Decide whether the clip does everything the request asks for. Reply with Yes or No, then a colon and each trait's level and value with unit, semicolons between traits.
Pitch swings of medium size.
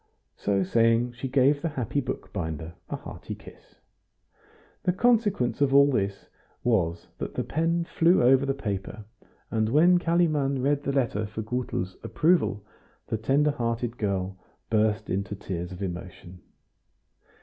No: wide, 6.3 semitones